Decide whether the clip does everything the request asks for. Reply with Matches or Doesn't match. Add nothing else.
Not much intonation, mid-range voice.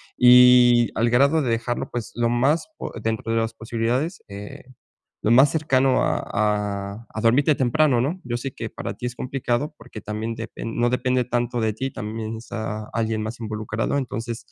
Doesn't match